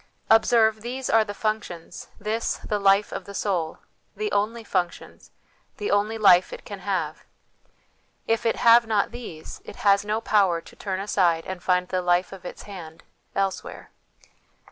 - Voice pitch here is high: Yes, high, 200 Hz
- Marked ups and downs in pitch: No, average, 3.4 semitones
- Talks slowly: No, average, 165 wpm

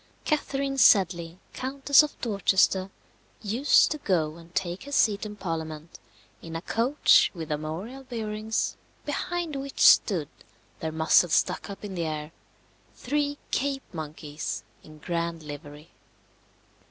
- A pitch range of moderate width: No, wide, 8.6 semitones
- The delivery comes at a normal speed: No, slow, 130 wpm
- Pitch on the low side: No, high, 190 Hz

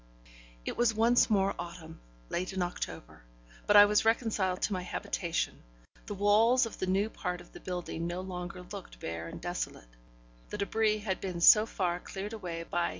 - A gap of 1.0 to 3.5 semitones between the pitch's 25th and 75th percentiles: Yes, average, 3.2 semitones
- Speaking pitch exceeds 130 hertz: Yes, medium, 185 Hz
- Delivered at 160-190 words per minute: Yes, average, 185 wpm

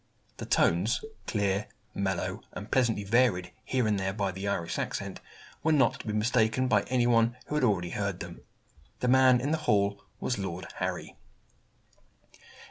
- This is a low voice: Yes, low, 105 Hz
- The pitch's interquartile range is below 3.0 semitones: No, average, 4.3 semitones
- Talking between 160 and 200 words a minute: Yes, average, 165 wpm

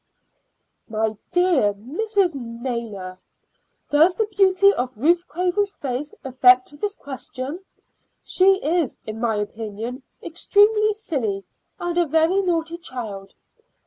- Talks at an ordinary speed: No, slow, 115 wpm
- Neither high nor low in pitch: No, very high, 290 Hz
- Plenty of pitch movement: Yes, wide, 7.7 semitones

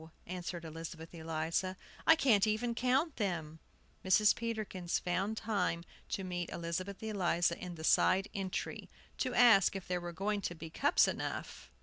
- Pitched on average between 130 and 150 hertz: No, medium, 185 Hz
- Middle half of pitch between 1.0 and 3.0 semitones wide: No, average, 3.9 semitones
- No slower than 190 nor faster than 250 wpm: No, average, 150 wpm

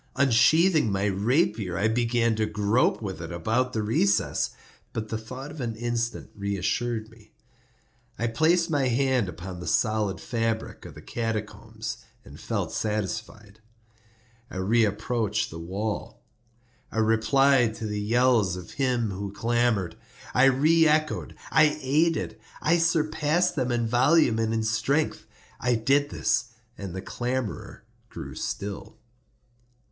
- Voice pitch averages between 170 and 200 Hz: No, low, 115 Hz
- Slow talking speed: Yes, slow, 130 wpm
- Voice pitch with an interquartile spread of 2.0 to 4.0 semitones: Yes, average, 3.7 semitones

